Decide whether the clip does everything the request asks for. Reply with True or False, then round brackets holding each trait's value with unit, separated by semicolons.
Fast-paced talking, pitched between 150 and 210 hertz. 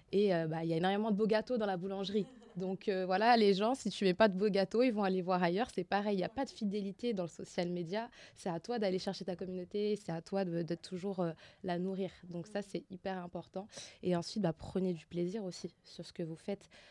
True (270 wpm; 190 Hz)